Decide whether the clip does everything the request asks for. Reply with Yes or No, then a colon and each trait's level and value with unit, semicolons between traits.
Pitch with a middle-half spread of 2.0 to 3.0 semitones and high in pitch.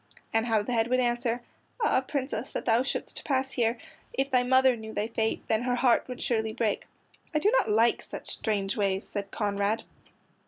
Yes: narrow, 2.6 semitones; high, 235 Hz